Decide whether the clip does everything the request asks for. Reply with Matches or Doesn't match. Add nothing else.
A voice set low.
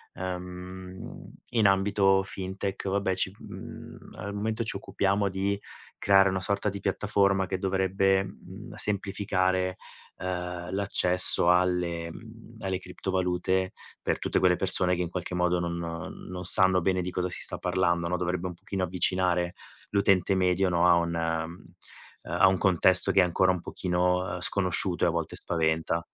Matches